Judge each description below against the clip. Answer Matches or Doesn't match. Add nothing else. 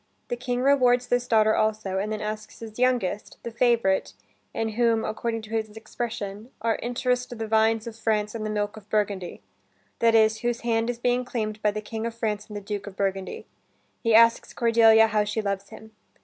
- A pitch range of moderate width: Doesn't match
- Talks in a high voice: Matches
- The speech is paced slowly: Doesn't match